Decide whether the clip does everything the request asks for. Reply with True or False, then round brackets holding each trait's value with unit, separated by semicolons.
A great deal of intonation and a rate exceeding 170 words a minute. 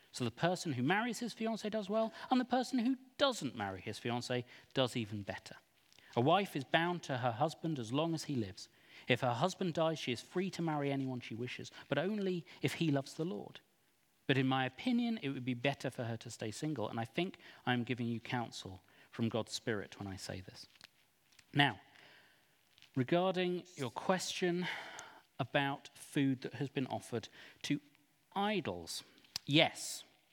True (6.5 semitones; 180 wpm)